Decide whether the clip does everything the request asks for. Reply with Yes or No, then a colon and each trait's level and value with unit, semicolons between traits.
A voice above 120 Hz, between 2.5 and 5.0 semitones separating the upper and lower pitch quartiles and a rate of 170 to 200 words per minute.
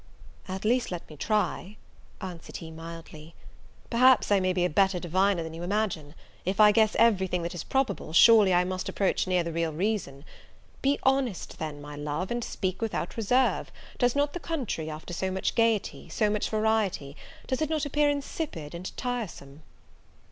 No: high, 190 Hz; wide, 5.4 semitones; average, 180 wpm